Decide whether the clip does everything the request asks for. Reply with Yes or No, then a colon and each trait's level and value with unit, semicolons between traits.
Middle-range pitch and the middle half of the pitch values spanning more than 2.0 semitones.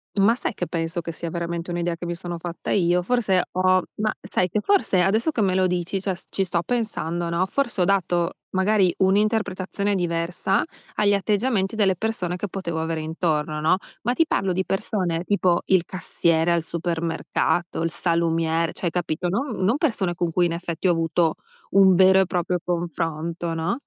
Yes: medium, 180 Hz; narrow, 2.5 semitones